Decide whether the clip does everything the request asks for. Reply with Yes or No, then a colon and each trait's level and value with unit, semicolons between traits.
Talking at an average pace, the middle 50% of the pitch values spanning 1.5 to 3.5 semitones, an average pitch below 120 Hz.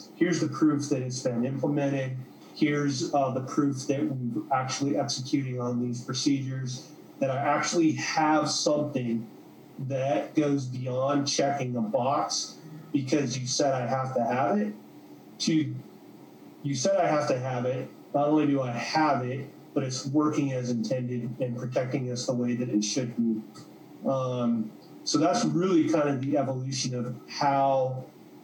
No: average, 160 wpm; narrow, 2.6 semitones; low, 135 Hz